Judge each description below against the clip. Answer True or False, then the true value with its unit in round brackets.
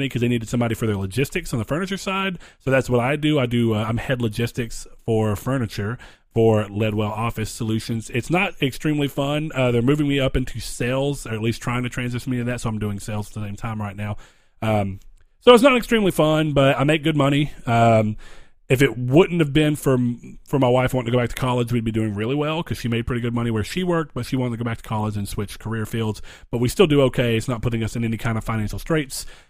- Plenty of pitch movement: False (3.8 semitones)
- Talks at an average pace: False (255 wpm)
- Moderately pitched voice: False (120 Hz)